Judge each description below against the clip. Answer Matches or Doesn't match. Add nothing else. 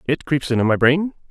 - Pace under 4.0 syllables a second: Doesn't match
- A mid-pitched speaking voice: Matches